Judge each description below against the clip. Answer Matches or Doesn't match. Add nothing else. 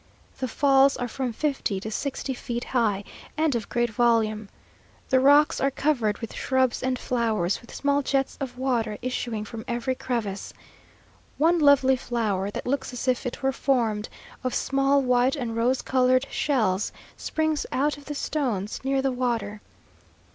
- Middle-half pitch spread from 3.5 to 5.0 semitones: Doesn't match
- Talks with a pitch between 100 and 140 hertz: Doesn't match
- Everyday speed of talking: Matches